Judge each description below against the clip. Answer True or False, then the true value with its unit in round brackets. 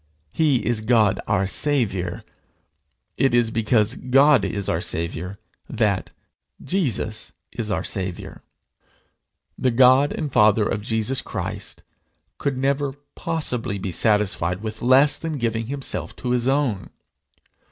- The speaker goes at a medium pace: False (125 wpm)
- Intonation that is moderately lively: True (4.6 semitones)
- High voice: False (115 Hz)